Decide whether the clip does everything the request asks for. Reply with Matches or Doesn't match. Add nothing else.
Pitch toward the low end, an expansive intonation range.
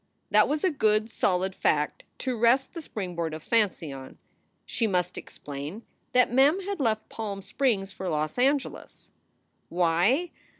Doesn't match